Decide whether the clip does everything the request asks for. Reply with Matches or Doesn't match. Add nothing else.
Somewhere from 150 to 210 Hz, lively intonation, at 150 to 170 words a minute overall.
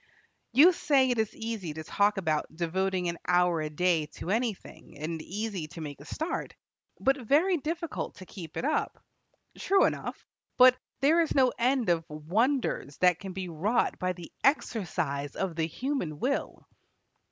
Matches